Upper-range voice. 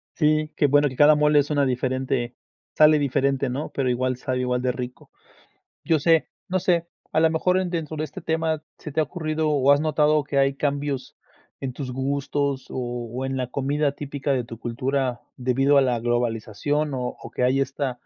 No: medium, 140 Hz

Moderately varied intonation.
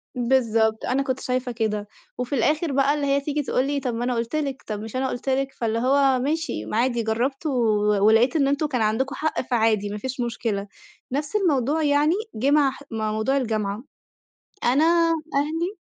Yes: average, 3.9 semitones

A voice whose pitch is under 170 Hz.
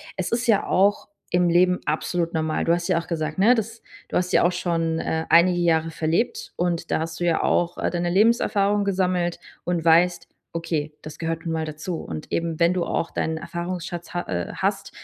No: medium, 175 Hz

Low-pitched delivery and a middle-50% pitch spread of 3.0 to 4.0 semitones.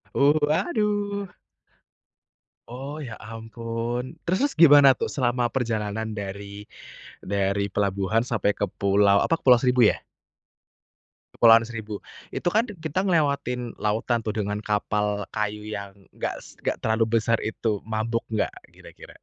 No: low, 115 Hz; average, 4.5 semitones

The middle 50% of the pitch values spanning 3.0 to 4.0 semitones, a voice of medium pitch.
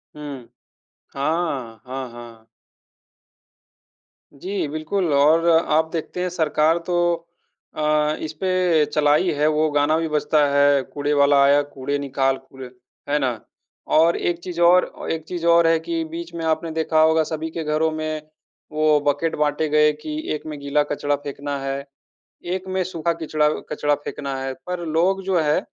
No: narrow, 2.5 semitones; medium, 155 Hz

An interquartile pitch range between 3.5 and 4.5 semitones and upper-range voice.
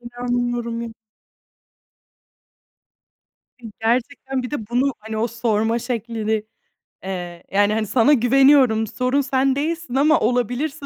No: average, 3.1 semitones; high, 240 Hz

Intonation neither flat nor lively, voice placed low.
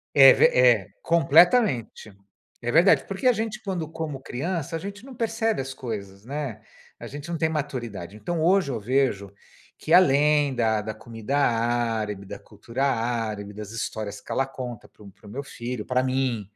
No: wide, 6.2 semitones; low, 130 Hz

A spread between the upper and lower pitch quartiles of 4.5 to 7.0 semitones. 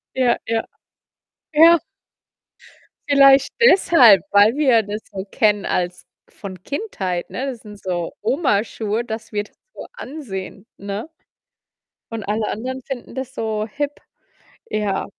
Yes: average, 4.8 semitones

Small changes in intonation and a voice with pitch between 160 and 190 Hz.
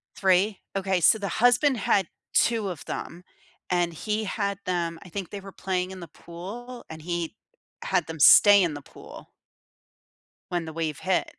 No: average, 3.1 semitones; medium, 185 Hz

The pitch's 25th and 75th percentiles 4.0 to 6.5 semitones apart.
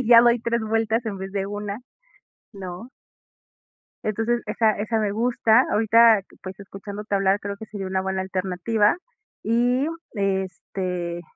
No: average, 2.9 semitones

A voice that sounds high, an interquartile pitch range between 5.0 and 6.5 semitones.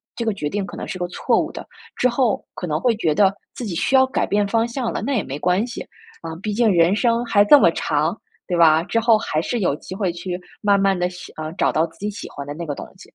Yes: high, 195 Hz; wide, 5.4 semitones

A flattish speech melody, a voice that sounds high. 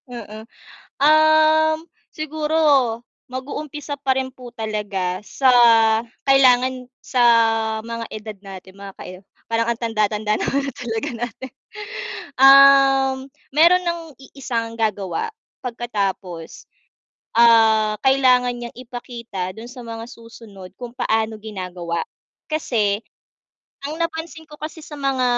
No: average, 4.1 semitones; high, 245 Hz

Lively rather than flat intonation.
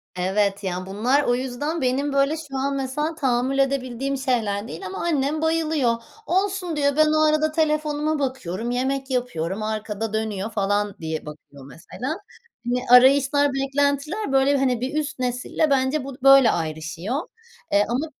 No: average, 4.9 semitones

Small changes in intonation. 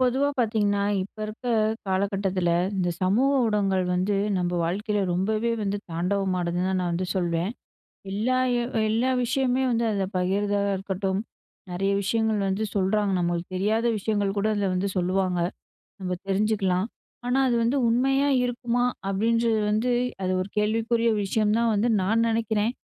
No: average, 3.3 semitones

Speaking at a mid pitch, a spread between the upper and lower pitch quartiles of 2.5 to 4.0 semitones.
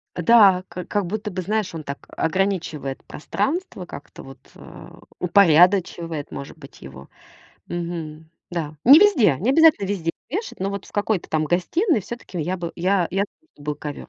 No: medium, 180 Hz; average, 4.6 semitones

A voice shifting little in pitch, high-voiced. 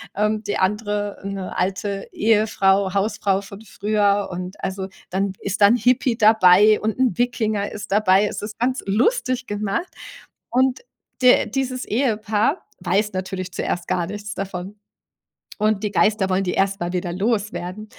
Yes: narrow, 2.1 semitones; high, 205 Hz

